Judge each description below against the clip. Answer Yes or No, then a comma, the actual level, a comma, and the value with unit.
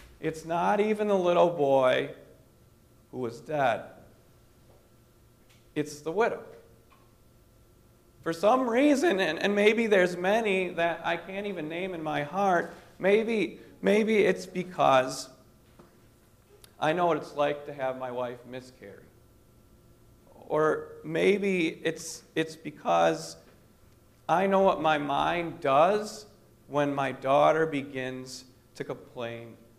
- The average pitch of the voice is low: No, medium, 145 Hz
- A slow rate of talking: Yes, slow, 120 wpm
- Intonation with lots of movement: Yes, wide, 7.0 semitones